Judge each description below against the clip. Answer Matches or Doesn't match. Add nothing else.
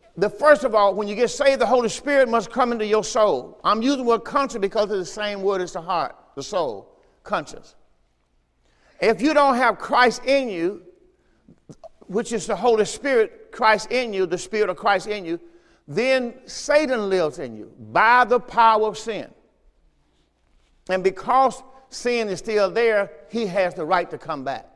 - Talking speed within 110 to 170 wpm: Doesn't match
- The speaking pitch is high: Matches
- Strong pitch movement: Doesn't match